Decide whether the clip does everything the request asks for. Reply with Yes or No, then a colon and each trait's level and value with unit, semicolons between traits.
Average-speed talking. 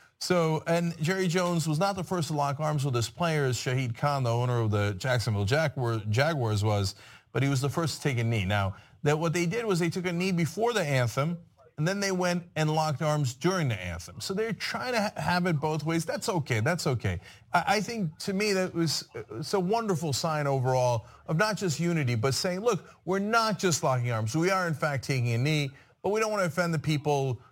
No: fast, 230 wpm